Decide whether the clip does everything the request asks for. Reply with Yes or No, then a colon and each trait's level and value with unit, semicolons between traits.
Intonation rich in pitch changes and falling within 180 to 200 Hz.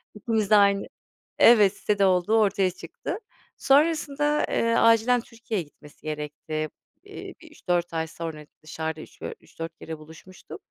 Yes: wide, 6.1 semitones; high, 190 Hz